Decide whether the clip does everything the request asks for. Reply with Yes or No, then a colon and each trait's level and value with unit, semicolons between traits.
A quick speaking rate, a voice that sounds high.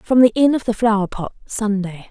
Yes: fast, 230 wpm; high, 220 Hz